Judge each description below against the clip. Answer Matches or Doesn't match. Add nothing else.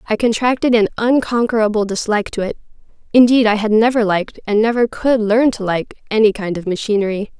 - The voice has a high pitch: Matches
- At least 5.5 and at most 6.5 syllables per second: Matches